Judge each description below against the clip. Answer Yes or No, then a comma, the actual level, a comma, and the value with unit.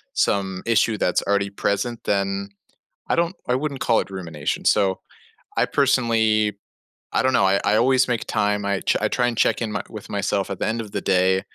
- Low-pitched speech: Yes, low, 105 Hz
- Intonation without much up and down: No, average, 3.0 semitones